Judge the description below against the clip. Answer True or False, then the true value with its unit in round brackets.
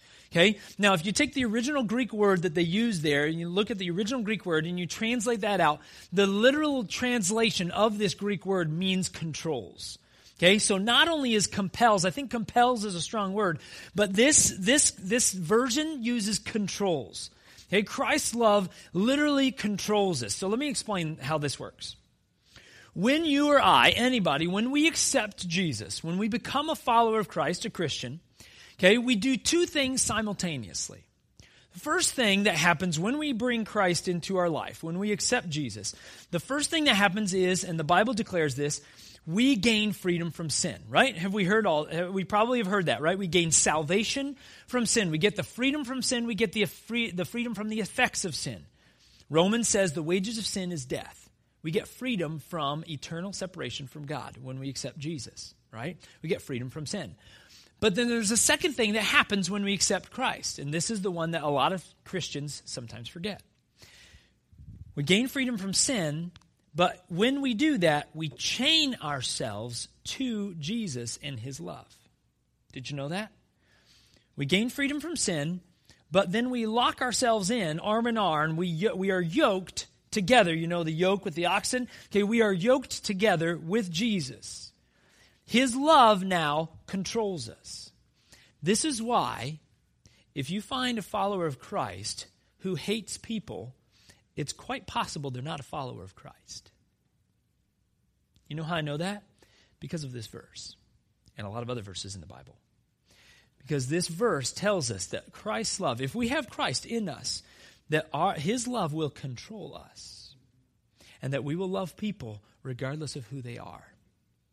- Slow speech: False (180 wpm)